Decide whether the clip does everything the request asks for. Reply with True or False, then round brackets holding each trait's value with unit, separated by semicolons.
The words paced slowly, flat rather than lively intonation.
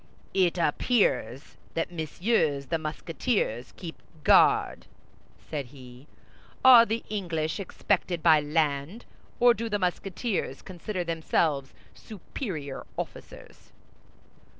False (100 wpm; 5.6 semitones)